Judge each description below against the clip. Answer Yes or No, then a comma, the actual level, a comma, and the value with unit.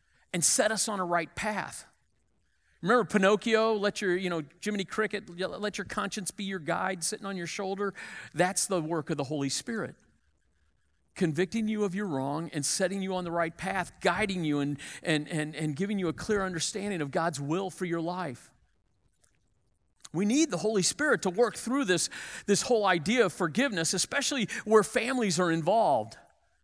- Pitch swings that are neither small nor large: Yes, average, 4.0 semitones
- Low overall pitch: No, medium, 185 Hz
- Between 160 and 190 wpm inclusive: Yes, average, 180 wpm